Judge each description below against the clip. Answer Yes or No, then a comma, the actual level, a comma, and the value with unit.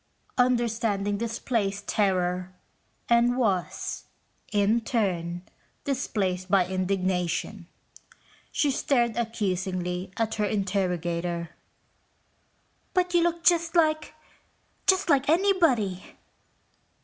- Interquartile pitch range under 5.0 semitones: No, average, 5.3 semitones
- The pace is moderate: No, slow, 85 wpm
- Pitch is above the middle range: Yes, high, 205 Hz